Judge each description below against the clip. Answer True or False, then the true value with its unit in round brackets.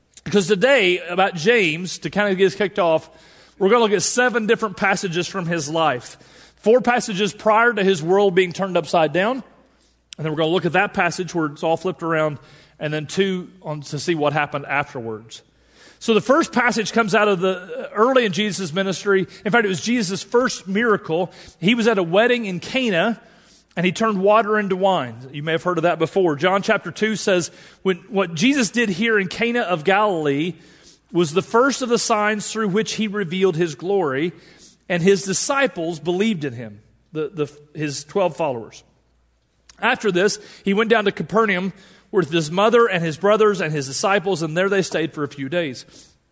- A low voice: False (190 Hz)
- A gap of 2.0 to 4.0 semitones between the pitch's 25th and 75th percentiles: False (4.5 semitones)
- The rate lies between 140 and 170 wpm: False (200 wpm)